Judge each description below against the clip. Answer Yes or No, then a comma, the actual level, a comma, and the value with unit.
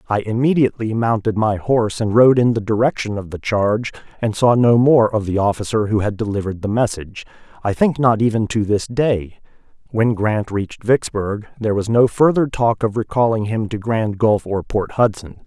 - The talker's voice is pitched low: Yes, low, 110 Hz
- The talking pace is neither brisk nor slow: Yes, average, 195 wpm